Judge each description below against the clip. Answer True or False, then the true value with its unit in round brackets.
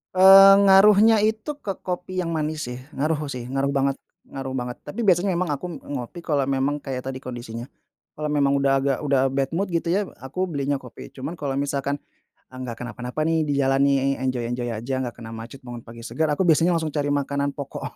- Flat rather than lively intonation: False (4.2 semitones)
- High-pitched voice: False (140 Hz)